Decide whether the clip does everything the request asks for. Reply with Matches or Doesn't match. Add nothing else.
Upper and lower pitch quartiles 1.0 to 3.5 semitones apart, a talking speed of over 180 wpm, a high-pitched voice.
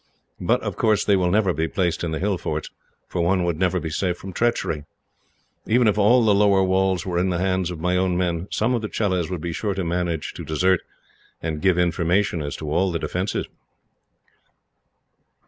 Doesn't match